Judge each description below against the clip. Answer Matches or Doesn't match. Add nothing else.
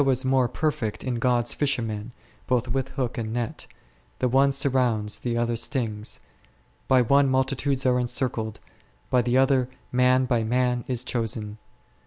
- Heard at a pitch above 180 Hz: Doesn't match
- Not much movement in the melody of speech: Matches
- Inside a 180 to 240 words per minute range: Doesn't match